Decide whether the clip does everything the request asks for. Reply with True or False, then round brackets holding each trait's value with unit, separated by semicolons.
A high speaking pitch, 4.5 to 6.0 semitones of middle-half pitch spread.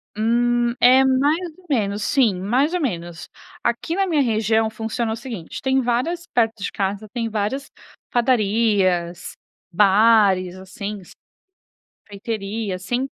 False (225 Hz; 4.1 semitones)